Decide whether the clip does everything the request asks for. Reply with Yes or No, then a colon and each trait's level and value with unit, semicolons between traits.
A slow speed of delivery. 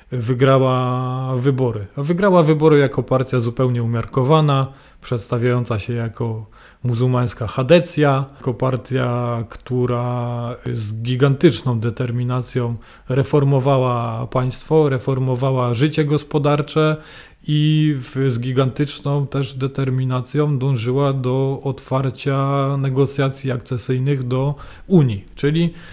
Yes: slow, 85 wpm